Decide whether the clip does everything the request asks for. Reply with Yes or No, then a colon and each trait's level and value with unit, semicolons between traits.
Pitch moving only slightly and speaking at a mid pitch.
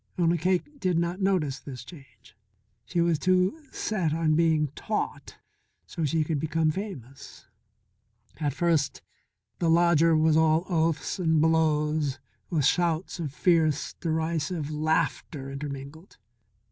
Yes: narrow, 2.3 semitones; medium, 160 Hz